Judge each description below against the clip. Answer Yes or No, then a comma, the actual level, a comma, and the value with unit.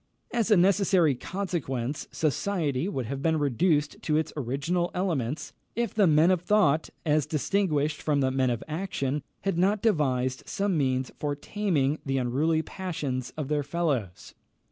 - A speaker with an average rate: Yes, average, 155 wpm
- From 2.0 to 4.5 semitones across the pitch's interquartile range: No, average, 5.1 semitones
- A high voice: No, medium, 155 Hz